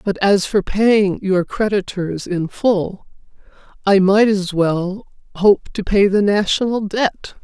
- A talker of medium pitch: No, high, 200 Hz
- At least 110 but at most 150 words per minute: Yes, average, 145 wpm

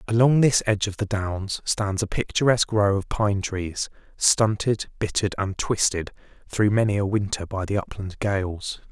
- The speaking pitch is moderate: No, low, 100 Hz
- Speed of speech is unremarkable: Yes, average, 170 wpm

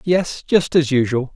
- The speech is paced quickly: No, average, 175 wpm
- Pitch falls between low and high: Yes, medium, 150 Hz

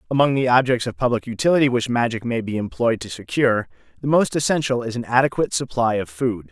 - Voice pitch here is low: Yes, low, 120 Hz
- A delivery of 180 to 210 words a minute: Yes, average, 200 wpm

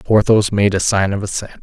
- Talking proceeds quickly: Yes, fast, 220 wpm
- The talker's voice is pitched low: Yes, low, 100 Hz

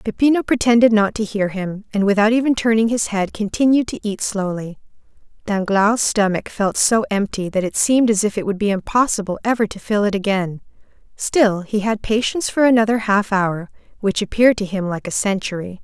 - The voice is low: No, high, 210 Hz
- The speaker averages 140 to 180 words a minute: No, average, 190 wpm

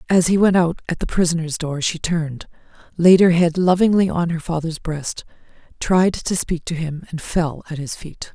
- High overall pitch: No, medium, 170 Hz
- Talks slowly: No, average, 200 wpm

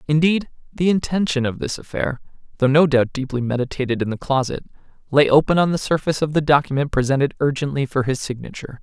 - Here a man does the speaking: Yes, male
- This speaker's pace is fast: No, average, 185 wpm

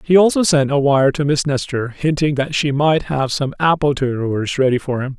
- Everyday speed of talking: No, fast, 220 wpm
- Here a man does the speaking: Yes, male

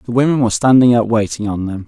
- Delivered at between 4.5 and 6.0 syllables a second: No, 6.9 syllables/s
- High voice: No, low, 115 Hz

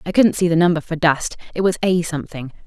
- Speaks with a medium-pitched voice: Yes, medium, 170 Hz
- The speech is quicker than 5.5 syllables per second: Yes, 6.3 syllables/s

